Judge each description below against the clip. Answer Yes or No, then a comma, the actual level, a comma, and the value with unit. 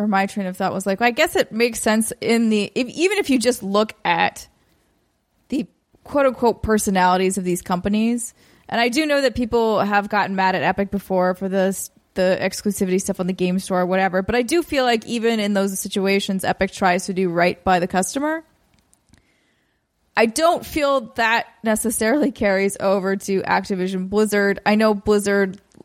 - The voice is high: Yes, high, 205 Hz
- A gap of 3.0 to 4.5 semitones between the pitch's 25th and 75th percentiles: Yes, average, 3.4 semitones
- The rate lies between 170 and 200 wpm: Yes, average, 190 wpm